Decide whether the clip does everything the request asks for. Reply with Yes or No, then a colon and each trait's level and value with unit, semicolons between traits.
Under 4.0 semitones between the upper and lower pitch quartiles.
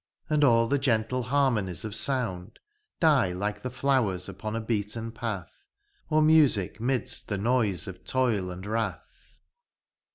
No: average, 4.4 semitones